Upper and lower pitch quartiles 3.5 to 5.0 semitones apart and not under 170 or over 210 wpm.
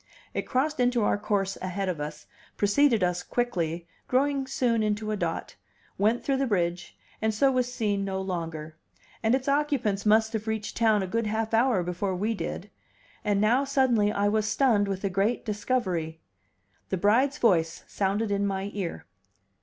Yes: average, 3.9 semitones; average, 175 wpm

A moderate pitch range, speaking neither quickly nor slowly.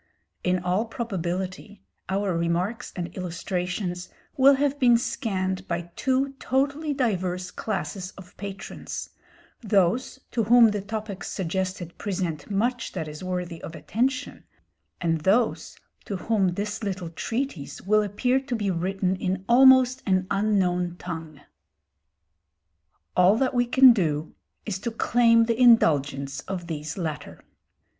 No: average, 4.7 semitones; slow, 130 wpm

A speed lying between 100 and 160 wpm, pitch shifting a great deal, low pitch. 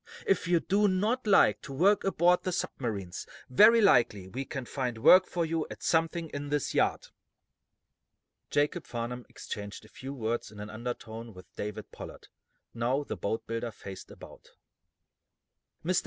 Yes: average, 155 wpm; wide, 7.7 semitones; low, 130 Hz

